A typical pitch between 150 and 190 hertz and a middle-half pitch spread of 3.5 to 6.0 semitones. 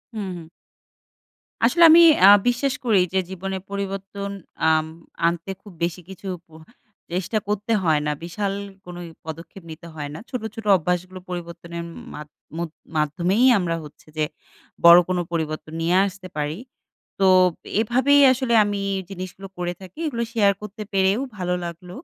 No: medium, 185 Hz; average, 2.8 semitones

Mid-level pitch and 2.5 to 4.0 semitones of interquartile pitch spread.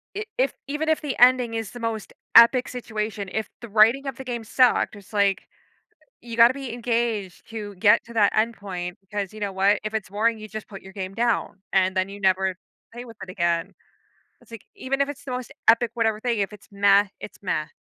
No: high, 220 Hz; average, 3.1 semitones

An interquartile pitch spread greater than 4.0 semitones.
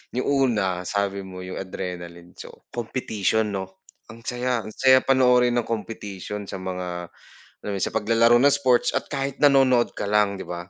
Yes: average, 4.7 semitones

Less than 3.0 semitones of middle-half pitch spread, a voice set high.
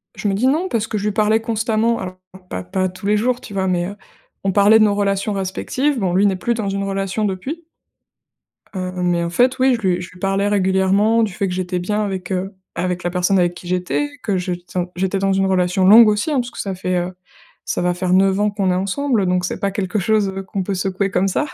Yes: narrow, 2.5 semitones; high, 195 Hz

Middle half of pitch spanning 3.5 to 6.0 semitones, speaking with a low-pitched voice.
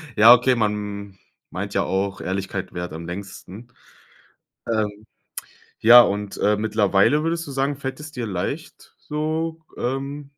Yes: wide, 5.5 semitones; low, 110 Hz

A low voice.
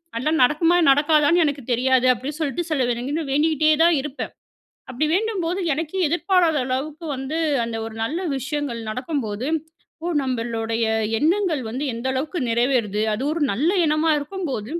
No: very high, 290 Hz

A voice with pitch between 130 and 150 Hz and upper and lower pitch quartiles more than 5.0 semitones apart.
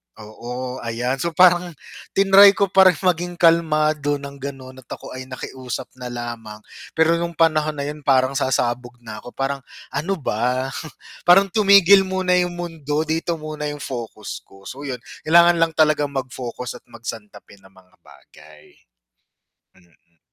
Yes: medium, 140 Hz; wide, 5.4 semitones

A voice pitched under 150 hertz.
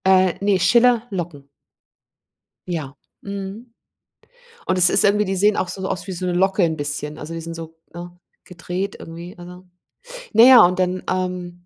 No: medium, 180 Hz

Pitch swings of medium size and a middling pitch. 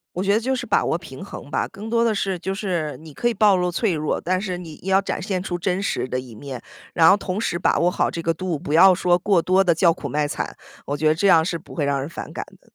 Yes: average, 3.4 semitones; medium, 180 Hz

